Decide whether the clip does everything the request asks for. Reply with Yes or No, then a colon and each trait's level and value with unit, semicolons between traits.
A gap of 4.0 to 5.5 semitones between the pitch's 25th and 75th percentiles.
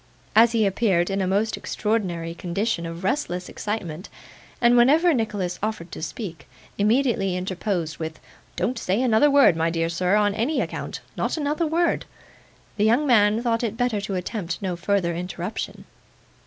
Yes: average, 4.6 semitones